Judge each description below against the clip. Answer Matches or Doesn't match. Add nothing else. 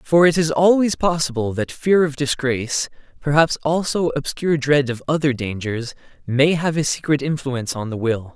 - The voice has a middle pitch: Matches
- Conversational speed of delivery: Matches